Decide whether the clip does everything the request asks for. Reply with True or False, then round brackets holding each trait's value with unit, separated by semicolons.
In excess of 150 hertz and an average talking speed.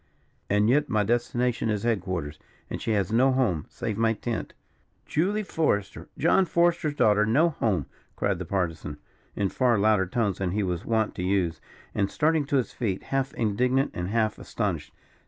False (110 Hz; 175 wpm)